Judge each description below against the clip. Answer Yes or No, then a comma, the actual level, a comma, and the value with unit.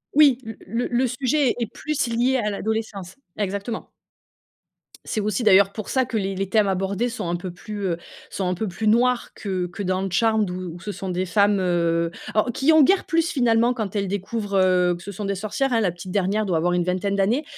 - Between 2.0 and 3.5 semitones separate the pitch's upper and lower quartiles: No, average, 4.0 semitones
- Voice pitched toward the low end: No, high, 205 Hz